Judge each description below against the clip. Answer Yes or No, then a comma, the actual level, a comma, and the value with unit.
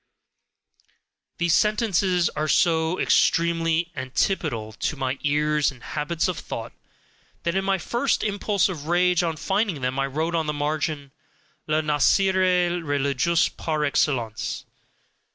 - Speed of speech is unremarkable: No, slow, 130 wpm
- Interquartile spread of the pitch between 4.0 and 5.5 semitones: No, average, 3.6 semitones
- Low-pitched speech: No, medium, 160 Hz